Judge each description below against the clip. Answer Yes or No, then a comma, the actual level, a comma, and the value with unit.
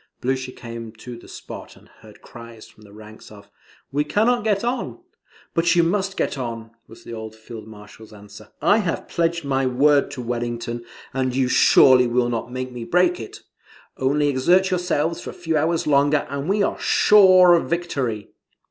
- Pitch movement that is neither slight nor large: No, wide, 6.4 semitones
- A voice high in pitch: No, low, 130 Hz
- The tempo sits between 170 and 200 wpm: Yes, average, 185 wpm